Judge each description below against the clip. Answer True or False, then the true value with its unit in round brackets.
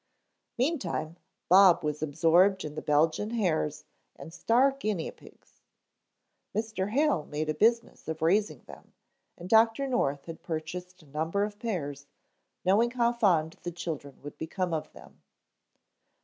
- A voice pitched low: False (180 Hz)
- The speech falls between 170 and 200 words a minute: False (140 wpm)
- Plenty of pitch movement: True (5.9 semitones)